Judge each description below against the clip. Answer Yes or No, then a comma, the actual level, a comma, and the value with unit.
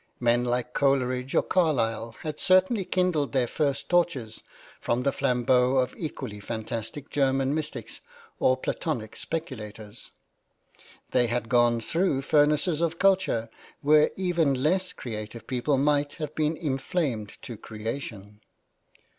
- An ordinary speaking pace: No, slow, 125 wpm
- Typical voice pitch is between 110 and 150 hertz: Yes, low, 135 Hz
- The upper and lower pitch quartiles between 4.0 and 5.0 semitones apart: Yes, average, 4.6 semitones